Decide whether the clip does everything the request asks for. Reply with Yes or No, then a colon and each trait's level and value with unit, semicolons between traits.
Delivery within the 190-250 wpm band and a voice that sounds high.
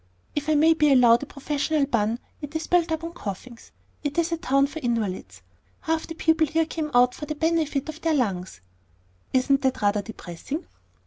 Yes: average, 195 wpm; very high, 285 Hz